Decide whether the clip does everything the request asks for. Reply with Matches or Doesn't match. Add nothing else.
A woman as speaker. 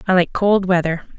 Matches